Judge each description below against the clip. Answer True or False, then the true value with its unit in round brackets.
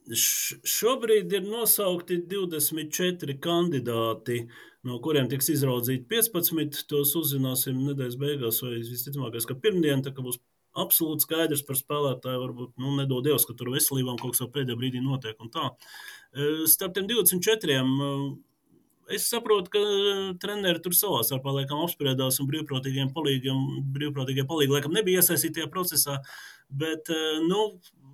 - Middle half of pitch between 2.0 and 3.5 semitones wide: False (4.6 semitones)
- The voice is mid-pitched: True (145 Hz)